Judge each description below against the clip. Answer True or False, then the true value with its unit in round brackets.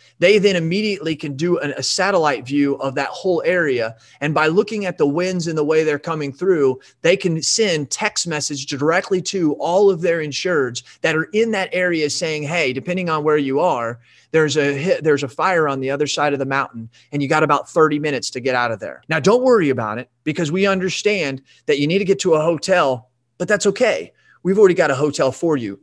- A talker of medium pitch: True (155 Hz)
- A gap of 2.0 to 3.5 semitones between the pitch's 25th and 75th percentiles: False (4.5 semitones)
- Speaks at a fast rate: True (230 wpm)